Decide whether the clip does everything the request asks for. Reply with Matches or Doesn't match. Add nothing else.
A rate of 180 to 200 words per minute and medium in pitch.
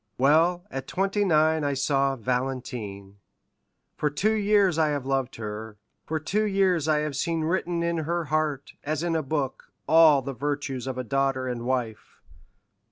Doesn't match